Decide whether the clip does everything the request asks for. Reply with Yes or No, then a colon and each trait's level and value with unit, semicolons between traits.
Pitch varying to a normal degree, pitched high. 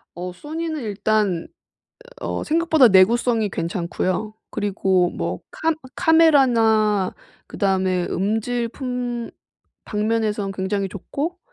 Yes: average, 4.6 semitones; high, 215 Hz